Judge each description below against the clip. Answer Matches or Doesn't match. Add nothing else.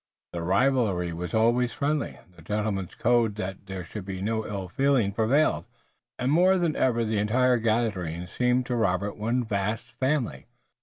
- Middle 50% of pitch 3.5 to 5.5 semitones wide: Matches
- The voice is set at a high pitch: Doesn't match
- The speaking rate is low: Doesn't match